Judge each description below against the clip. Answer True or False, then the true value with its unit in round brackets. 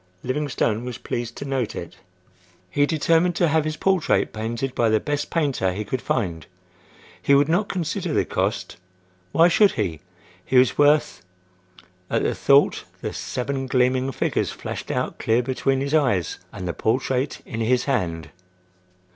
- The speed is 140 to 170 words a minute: True (155 wpm)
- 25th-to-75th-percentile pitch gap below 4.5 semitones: False (5.1 semitones)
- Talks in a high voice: False (130 Hz)